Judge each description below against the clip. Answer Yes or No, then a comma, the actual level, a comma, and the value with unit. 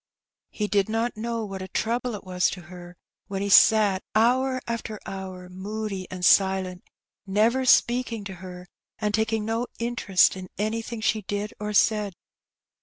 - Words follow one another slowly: No, average, 160 wpm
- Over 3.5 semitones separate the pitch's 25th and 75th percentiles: No, average, 3.1 semitones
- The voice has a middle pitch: No, high, 210 Hz